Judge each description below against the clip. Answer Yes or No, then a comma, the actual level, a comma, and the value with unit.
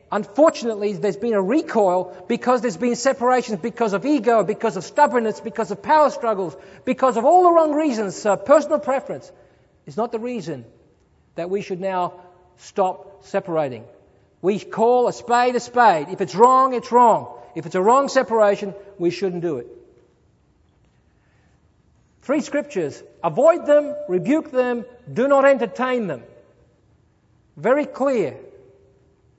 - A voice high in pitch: Yes, high, 230 Hz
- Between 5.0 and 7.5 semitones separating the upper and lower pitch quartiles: Yes, wide, 5.6 semitones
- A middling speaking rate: Yes, average, 145 wpm